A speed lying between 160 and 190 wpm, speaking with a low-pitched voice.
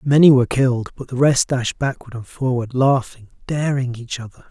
Yes: average, 185 wpm; low, 130 Hz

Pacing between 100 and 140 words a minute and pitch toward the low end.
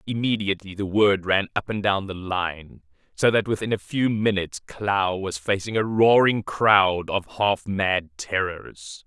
No: average, 165 wpm; low, 100 Hz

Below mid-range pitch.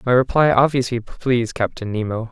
Yes: low, 120 Hz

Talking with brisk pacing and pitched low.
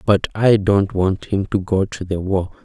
Yes: fast, 225 wpm; very low, 95 Hz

